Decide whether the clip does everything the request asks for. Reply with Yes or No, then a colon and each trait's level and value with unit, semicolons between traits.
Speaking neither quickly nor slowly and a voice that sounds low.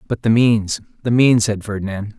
Yes: average, 165 wpm; low, 110 Hz